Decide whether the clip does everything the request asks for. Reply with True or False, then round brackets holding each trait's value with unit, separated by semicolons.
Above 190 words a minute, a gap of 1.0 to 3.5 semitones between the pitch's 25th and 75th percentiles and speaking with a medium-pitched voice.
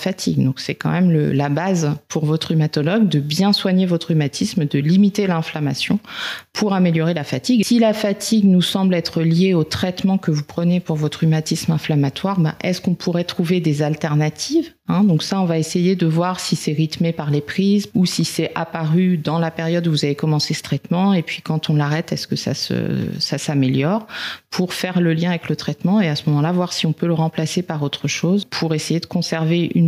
True (220 wpm; 3.2 semitones; 170 Hz)